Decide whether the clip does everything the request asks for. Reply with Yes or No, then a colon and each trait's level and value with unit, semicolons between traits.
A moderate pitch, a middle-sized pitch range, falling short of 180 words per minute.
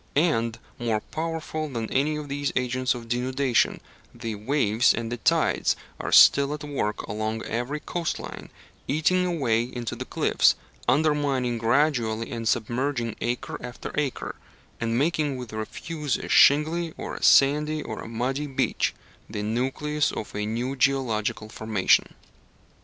No: low, 130 Hz; average, 4.4 semitones; average, 145 wpm